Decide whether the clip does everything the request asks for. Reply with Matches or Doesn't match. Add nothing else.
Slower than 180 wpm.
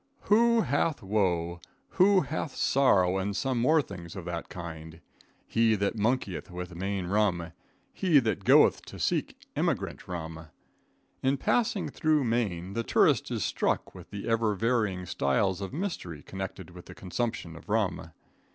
Matches